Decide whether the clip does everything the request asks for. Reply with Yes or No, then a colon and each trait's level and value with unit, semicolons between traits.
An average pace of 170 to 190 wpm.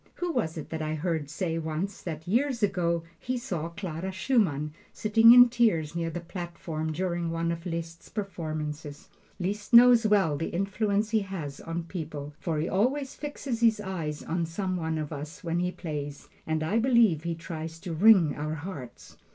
Yes: average, 180 wpm